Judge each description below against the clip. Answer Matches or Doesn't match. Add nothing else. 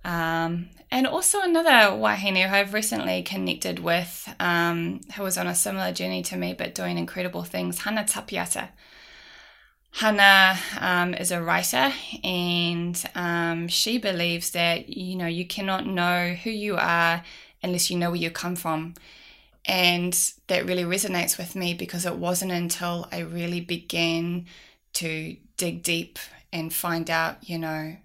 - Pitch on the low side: Doesn't match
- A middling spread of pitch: Doesn't match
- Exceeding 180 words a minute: Doesn't match